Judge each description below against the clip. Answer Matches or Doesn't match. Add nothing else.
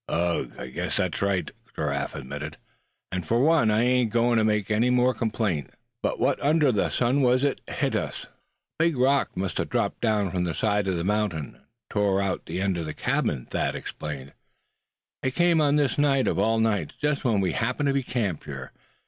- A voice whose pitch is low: Matches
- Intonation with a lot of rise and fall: Matches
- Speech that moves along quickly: Matches